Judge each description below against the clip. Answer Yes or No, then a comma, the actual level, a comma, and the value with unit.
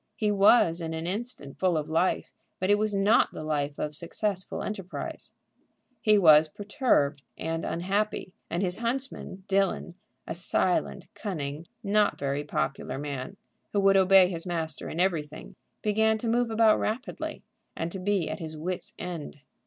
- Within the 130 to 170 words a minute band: Yes, average, 160 wpm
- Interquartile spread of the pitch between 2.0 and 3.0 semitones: No, average, 4.6 semitones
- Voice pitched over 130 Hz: Yes, medium, 185 Hz